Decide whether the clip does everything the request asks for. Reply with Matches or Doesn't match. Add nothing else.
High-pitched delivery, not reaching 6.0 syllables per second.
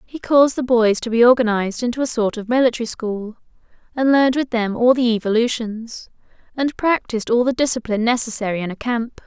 Doesn't match